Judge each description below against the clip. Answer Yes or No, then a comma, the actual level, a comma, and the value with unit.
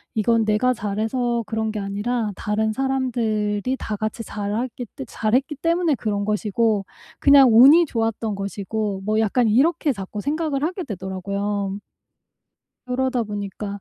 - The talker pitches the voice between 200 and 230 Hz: Yes, high, 220 Hz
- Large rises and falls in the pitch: No, average, 3.7 semitones